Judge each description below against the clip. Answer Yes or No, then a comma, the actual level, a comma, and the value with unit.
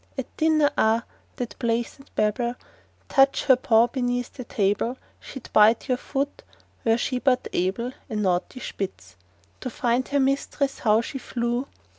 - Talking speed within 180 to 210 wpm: No, average, 140 wpm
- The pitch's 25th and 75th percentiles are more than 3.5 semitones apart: No, average, 2.9 semitones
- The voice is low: No, high, 245 Hz